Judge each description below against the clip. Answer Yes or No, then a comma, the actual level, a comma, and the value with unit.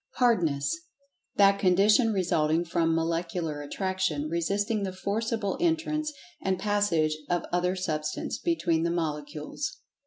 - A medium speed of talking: No, slow, 115 wpm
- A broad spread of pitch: No, average, 4.0 semitones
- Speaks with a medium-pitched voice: Yes, medium, 180 Hz